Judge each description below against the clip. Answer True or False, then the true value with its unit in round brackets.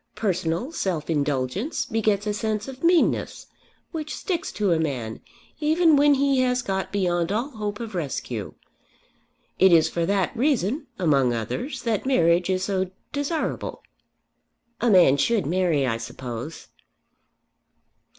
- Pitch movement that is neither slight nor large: False (7.7 semitones)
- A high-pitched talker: True (195 Hz)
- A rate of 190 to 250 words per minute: False (135 wpm)